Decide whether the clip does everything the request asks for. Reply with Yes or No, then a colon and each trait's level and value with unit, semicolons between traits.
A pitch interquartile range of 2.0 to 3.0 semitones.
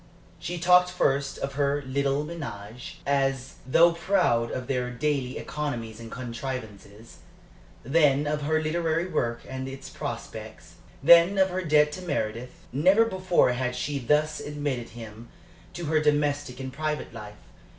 No: average, 3.9 semitones